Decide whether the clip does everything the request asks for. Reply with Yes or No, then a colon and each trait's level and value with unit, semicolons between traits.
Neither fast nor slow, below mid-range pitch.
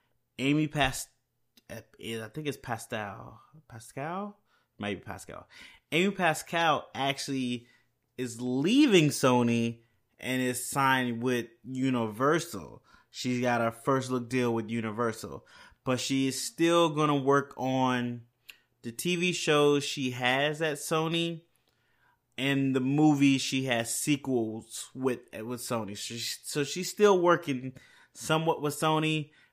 No: slow, 120 wpm; low, 130 Hz